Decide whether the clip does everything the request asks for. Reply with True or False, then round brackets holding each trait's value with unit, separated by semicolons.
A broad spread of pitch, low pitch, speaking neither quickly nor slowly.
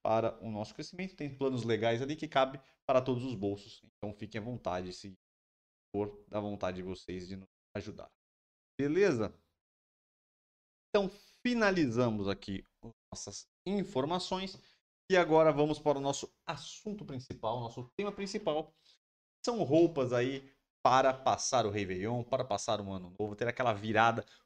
True (7.2 semitones; 120 Hz; 145 wpm)